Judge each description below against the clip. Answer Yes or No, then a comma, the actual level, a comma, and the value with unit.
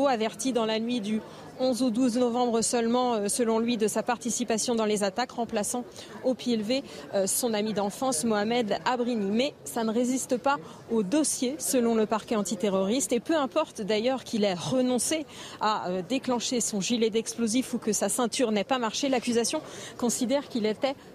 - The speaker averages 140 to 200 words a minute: Yes, average, 175 wpm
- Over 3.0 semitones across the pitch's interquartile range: No, average, 2.7 semitones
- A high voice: Yes, high, 240 Hz